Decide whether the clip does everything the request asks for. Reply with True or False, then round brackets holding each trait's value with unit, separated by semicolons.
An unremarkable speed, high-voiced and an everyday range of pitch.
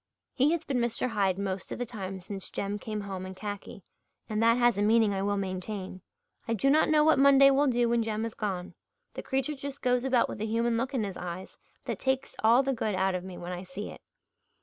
False (240 wpm; 220 Hz; 4.7 semitones)